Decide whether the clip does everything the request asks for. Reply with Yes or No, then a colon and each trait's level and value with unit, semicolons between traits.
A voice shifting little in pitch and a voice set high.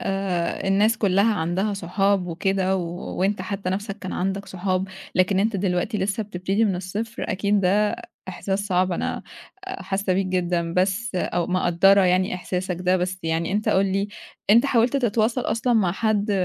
Yes: narrow, 2.2 semitones; high, 195 Hz